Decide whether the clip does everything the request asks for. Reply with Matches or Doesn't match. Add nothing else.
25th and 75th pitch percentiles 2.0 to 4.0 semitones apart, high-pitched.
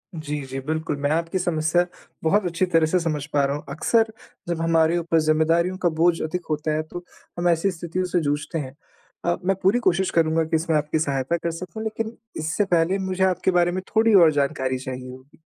Doesn't match